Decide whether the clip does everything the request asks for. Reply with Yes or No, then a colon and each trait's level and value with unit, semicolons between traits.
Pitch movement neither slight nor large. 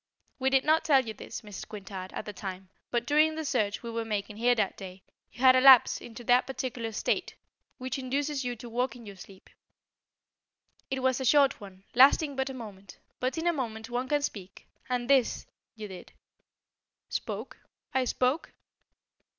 Yes: average, 4.0 semitones